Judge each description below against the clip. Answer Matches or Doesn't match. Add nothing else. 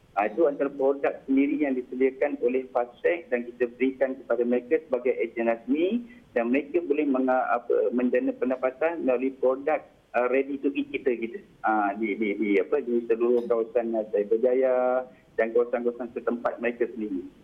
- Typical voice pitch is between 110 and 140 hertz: Matches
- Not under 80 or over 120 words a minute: Doesn't match